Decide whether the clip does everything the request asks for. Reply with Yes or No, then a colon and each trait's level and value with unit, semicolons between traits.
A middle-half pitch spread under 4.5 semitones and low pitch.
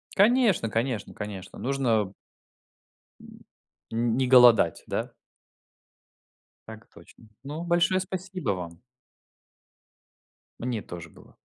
No: wide, 8.2 semitones; low, 120 Hz